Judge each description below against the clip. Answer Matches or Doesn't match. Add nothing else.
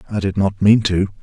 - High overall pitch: Doesn't match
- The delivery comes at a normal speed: Doesn't match